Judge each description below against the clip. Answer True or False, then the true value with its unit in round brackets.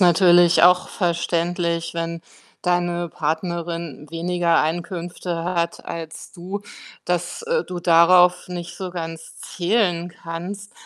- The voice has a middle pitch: True (175 Hz)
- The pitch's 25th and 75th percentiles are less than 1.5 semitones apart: True (1.1 semitones)